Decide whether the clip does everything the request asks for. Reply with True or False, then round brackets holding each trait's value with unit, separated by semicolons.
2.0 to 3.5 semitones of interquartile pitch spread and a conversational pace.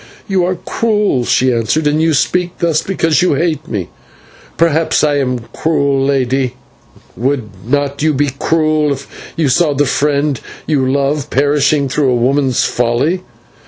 True (3.1 semitones; 155 wpm)